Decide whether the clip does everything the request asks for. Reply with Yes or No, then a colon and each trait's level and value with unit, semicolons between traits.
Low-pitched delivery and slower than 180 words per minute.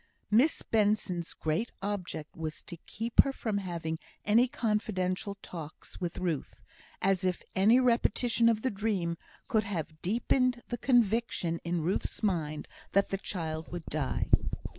No: high, 195 Hz; average, 140 wpm